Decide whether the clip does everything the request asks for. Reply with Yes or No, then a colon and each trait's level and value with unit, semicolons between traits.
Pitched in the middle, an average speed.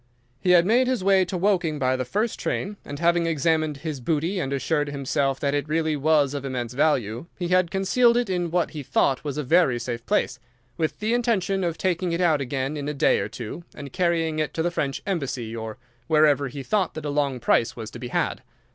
No: medium, 155 Hz; fast, 225 wpm